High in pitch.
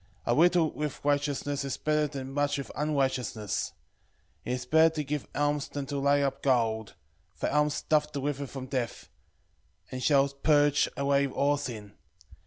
No: medium, 140 Hz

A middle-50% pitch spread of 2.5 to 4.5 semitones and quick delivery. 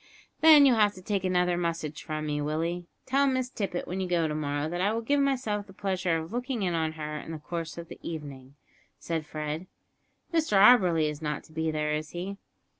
No: average, 4.9 semitones; fast, 220 wpm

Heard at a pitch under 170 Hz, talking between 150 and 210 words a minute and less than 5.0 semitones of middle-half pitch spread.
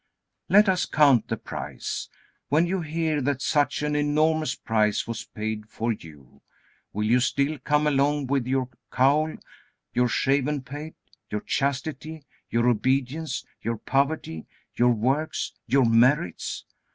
No: low, 135 Hz; slow, 135 wpm; average, 4.1 semitones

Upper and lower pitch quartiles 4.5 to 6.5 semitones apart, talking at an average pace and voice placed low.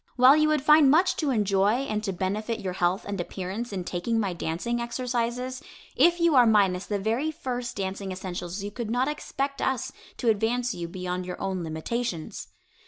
No: average, 5.0 semitones; average, 185 wpm; high, 220 Hz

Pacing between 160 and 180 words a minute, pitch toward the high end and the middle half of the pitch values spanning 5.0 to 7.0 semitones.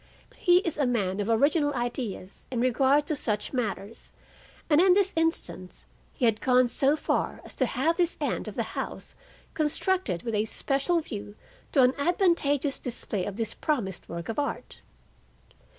Yes: average, 165 wpm; very high, 260 Hz; wide, 5.6 semitones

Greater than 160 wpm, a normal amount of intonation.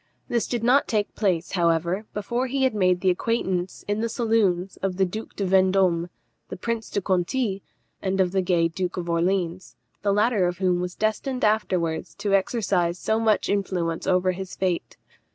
Yes: average, 180 wpm; average, 3.3 semitones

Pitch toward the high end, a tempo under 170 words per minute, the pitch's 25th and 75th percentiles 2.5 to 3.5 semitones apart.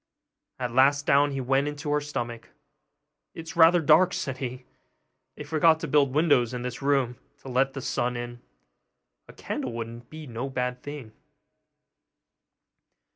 No: low, 135 Hz; average, 155 wpm; average, 3.1 semitones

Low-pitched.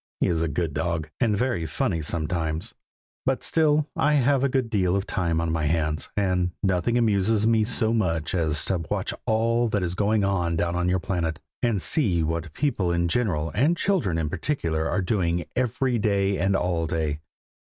Yes: very low, 90 Hz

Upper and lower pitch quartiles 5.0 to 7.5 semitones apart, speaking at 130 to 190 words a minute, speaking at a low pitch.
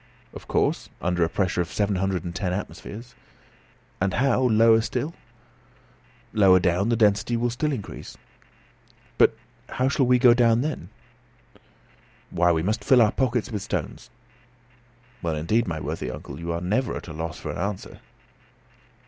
Yes: average, 5.3 semitones; average, 165 wpm; low, 105 Hz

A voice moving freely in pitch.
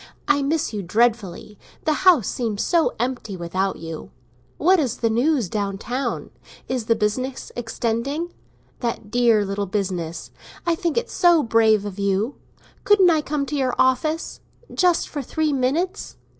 Yes: wide, 6.6 semitones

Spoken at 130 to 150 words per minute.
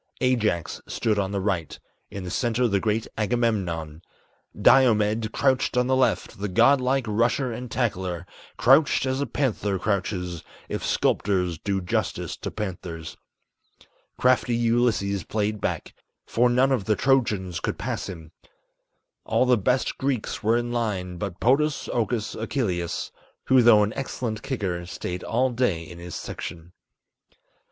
Yes: average, 145 wpm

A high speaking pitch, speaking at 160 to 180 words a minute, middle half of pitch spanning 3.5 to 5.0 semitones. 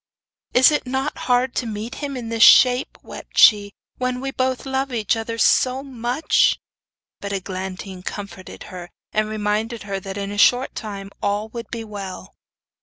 Yes: high, 225 Hz; average, 170 wpm; average, 3.9 semitones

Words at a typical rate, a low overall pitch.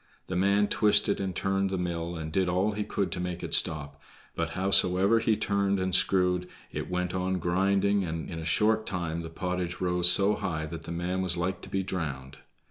No: fast, 210 wpm; very low, 90 Hz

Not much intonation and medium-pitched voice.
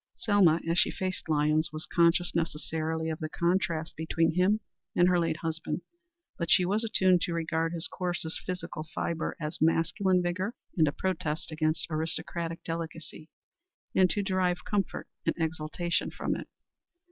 Yes: narrow, 2.1 semitones; medium, 165 Hz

